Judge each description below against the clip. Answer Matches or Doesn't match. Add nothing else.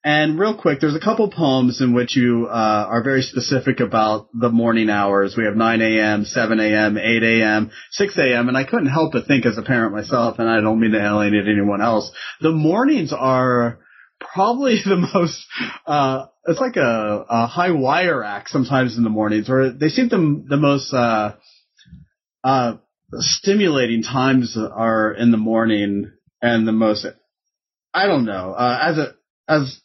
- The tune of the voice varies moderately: Matches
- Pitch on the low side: Matches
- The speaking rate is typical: Matches